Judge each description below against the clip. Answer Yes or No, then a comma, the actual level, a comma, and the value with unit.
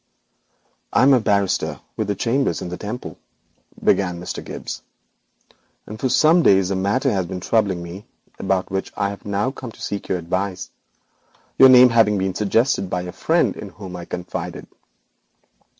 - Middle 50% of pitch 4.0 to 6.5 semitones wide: No, average, 3.5 semitones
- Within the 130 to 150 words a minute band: No, average, 165 wpm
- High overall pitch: No, low, 100 Hz